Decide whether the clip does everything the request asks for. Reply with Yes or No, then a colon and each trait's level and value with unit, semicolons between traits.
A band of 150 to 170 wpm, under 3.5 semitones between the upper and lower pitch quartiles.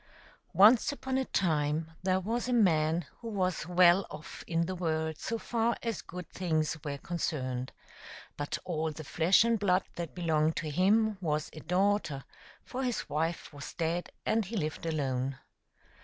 No: average, 165 wpm; average, 4.7 semitones